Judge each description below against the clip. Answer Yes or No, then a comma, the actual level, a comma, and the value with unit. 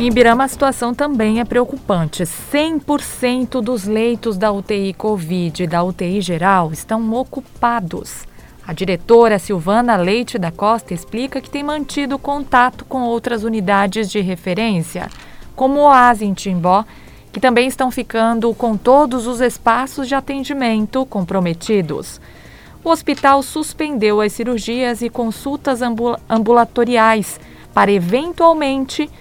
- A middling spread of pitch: Yes, average, 4.3 semitones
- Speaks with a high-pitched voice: Yes, high, 235 Hz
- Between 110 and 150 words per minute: Yes, average, 125 wpm